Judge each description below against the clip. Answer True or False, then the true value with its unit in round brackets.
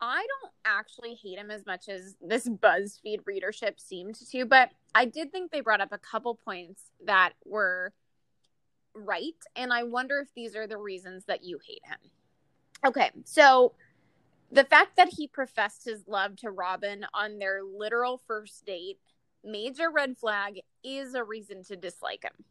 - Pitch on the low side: False (220 Hz)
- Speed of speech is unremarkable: True (170 wpm)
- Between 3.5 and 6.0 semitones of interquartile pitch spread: True (5.1 semitones)